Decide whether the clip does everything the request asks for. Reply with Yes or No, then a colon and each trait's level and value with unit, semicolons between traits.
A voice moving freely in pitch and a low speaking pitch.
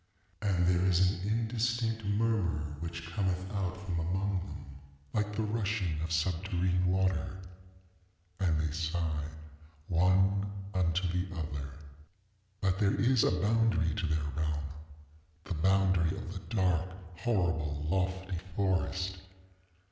No: average, 3.3 semitones; very low, 90 Hz